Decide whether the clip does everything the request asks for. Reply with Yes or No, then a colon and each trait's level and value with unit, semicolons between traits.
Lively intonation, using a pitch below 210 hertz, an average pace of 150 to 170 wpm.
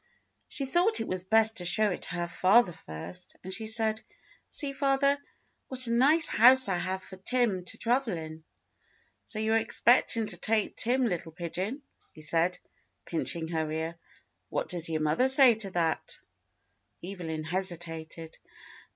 Yes: wide, 6.1 semitones; high, 190 Hz; average, 160 wpm